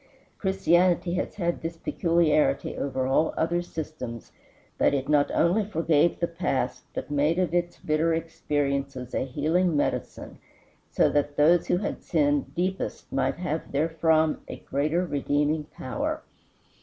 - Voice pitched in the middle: Yes, medium, 160 Hz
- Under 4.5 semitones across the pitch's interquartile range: Yes, average, 3.0 semitones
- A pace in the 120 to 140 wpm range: Yes, slow, 135 wpm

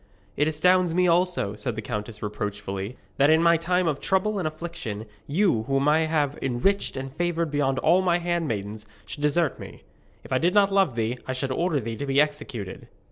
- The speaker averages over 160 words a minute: Yes, average, 195 wpm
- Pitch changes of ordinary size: No, wide, 6.1 semitones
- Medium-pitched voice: Yes, medium, 150 Hz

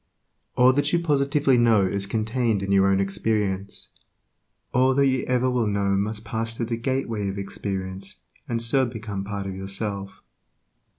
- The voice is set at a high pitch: No, low, 110 Hz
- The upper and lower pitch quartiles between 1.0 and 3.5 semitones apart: No, average, 4.2 semitones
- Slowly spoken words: No, average, 165 wpm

